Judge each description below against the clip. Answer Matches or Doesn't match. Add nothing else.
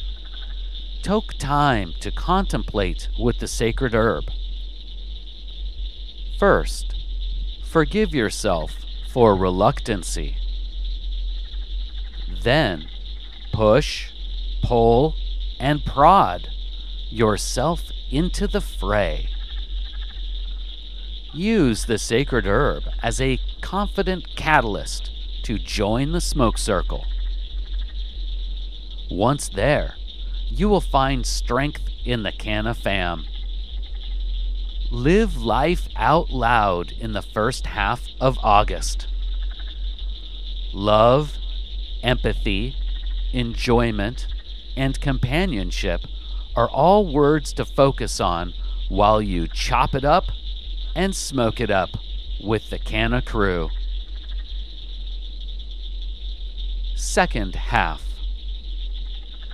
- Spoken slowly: Matches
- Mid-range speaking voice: Doesn't match